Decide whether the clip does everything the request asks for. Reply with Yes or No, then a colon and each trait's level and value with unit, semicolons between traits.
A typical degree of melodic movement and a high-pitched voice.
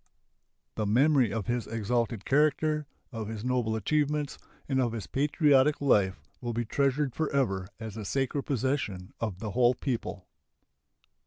No: average, 4.2 semitones; low, 125 Hz